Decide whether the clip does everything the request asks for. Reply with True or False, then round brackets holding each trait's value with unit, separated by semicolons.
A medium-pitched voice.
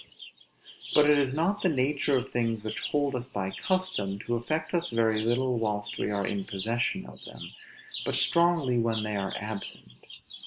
False (120 Hz)